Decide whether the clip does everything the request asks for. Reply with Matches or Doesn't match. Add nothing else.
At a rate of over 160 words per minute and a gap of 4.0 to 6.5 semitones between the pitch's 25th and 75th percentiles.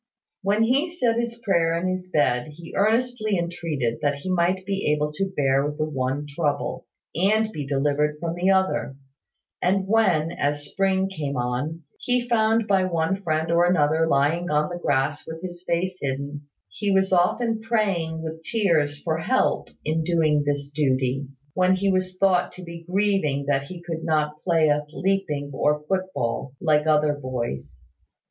Matches